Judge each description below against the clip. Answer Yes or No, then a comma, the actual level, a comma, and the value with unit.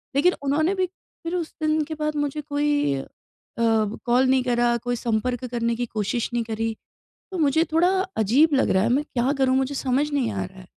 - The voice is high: Yes, very high, 260 Hz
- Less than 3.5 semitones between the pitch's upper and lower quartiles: No, average, 4.3 semitones